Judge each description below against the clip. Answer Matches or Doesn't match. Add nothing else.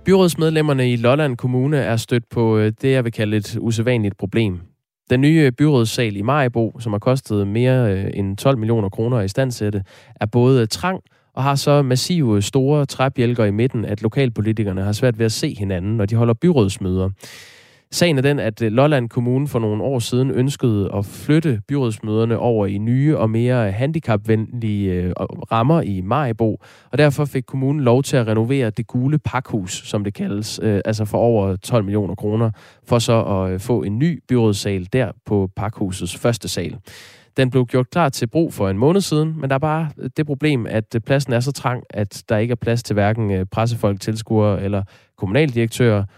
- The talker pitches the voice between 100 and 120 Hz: Matches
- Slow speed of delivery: Doesn't match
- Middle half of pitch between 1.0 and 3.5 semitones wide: Doesn't match